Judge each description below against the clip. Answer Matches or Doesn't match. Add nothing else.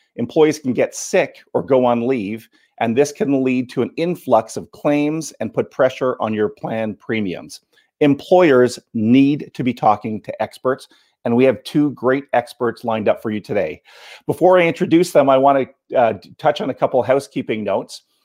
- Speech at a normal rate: Matches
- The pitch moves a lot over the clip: Doesn't match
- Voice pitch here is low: Matches